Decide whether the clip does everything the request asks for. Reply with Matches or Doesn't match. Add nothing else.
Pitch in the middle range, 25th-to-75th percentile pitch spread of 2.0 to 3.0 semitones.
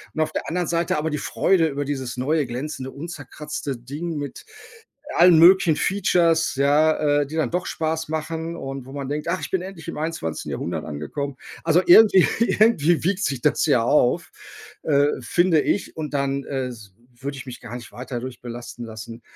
Doesn't match